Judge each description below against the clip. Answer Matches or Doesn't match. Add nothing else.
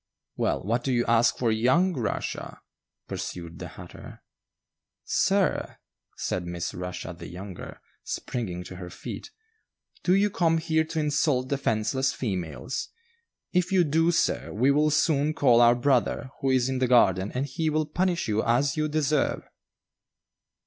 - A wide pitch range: Matches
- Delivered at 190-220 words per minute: Doesn't match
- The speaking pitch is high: Doesn't match